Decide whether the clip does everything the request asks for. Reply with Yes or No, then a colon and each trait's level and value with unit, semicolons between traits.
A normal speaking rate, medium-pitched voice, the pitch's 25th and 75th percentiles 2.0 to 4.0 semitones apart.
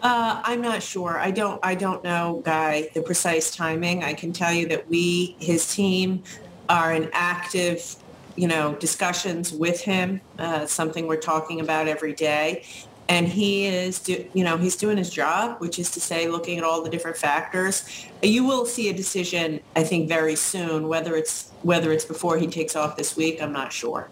Yes: average, 195 wpm; medium, 170 Hz; narrow, 2.4 semitones